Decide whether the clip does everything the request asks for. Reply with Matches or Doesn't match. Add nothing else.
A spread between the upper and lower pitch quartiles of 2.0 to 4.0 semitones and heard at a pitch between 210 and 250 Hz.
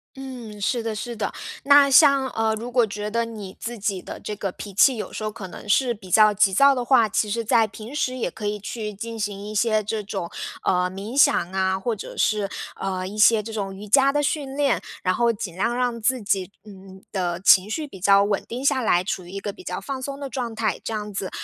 Matches